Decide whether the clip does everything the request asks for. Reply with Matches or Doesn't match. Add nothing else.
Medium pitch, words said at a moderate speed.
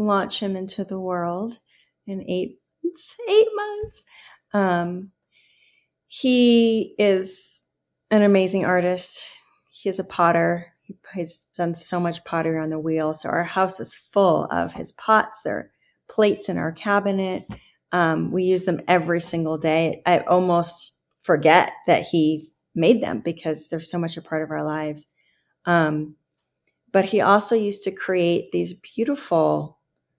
Matches